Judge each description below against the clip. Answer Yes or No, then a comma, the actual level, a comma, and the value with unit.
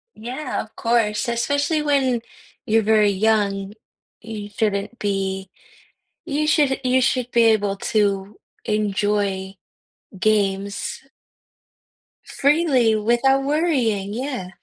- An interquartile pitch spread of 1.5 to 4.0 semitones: No, average, 4.4 semitones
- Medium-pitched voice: No, high, 220 Hz